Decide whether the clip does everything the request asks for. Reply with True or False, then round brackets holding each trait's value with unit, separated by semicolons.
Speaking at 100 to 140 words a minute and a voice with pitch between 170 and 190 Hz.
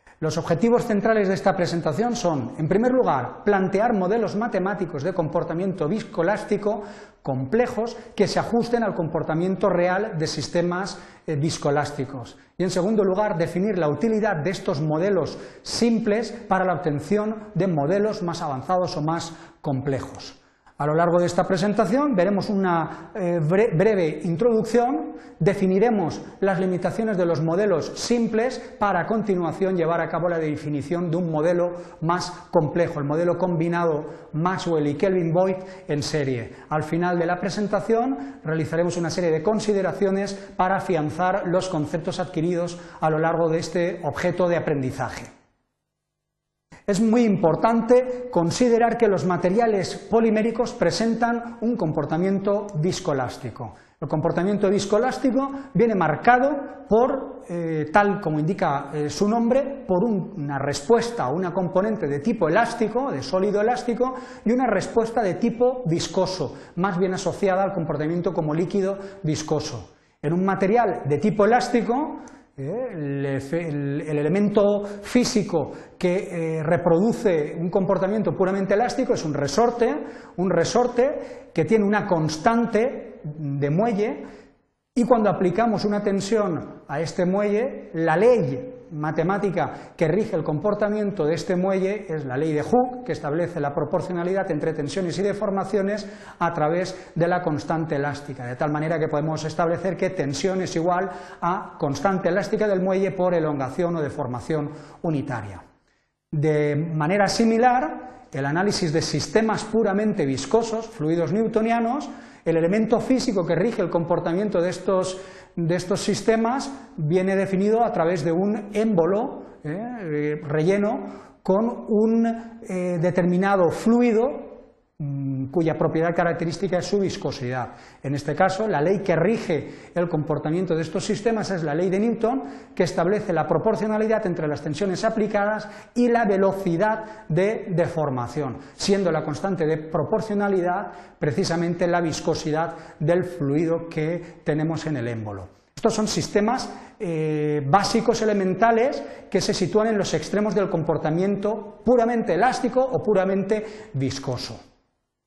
True (135 wpm; 185 Hz)